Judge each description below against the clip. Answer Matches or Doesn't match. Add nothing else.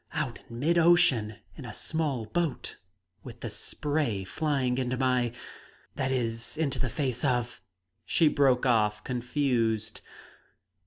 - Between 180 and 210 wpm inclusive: Doesn't match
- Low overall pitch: Matches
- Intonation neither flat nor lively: Matches